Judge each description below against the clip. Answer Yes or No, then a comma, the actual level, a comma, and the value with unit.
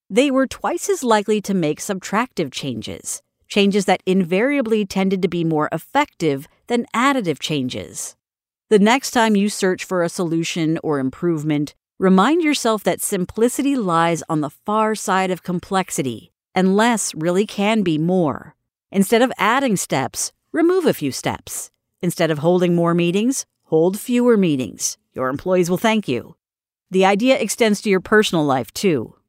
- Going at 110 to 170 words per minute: Yes, average, 155 wpm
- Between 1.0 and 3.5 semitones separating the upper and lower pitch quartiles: No, average, 5.3 semitones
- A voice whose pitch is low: No, high, 190 Hz